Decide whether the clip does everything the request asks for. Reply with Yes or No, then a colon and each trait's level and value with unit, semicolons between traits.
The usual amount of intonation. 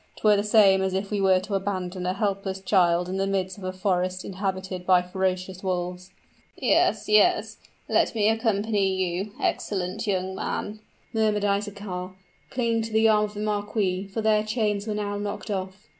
No: narrow, 2.1 semitones